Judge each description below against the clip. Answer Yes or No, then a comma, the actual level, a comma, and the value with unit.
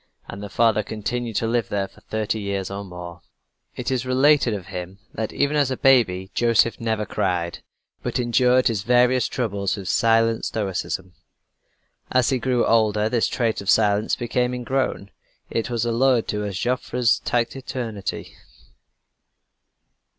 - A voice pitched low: Yes, low, 115 Hz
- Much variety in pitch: No, average, 3.5 semitones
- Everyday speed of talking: Yes, average, 150 wpm